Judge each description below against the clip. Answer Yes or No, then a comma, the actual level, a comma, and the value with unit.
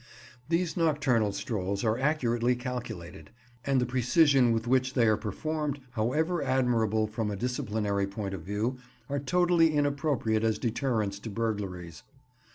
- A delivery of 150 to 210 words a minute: No, average, 140 wpm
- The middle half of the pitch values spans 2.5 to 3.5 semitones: No, average, 4.8 semitones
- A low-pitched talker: Yes, low, 120 Hz